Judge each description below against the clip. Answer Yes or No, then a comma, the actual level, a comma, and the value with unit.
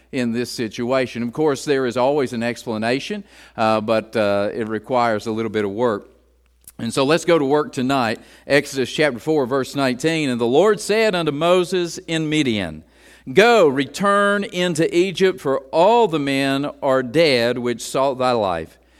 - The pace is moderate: Yes, average, 170 wpm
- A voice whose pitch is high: No, low, 135 Hz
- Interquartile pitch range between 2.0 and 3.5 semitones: No, average, 5.3 semitones